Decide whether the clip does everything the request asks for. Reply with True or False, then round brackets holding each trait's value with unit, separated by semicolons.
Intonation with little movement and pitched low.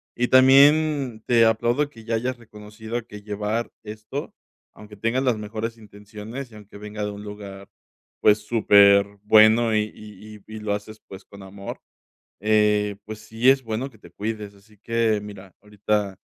True (1.8 semitones; 110 Hz)